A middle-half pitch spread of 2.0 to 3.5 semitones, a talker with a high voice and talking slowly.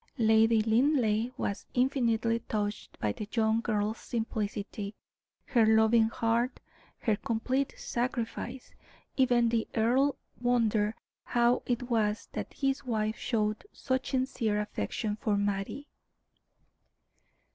Yes: narrow, 2.4 semitones; high, 225 Hz; slow, 110 wpm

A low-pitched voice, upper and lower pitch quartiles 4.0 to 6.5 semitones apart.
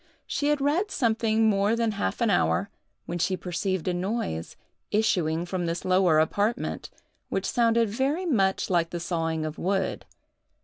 No: high, 195 Hz; average, 4.7 semitones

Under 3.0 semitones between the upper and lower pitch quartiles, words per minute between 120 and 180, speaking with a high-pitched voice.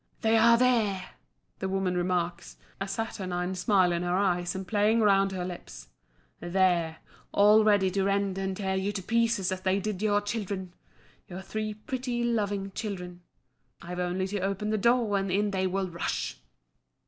Yes: narrow, 2.4 semitones; average, 170 wpm; high, 195 Hz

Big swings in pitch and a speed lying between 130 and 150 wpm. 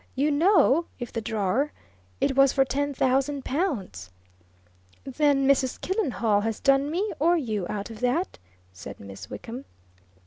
No: average, 4.6 semitones; average, 145 wpm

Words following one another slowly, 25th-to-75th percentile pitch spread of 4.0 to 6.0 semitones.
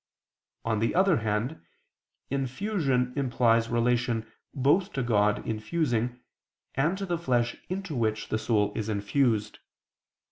Yes: slow, 120 wpm; average, 4.4 semitones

